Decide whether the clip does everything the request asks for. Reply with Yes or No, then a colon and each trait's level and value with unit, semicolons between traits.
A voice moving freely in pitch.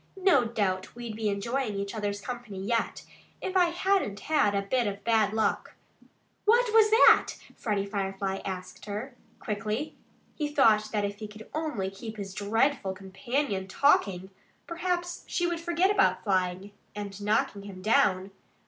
Yes: wide, 6.2 semitones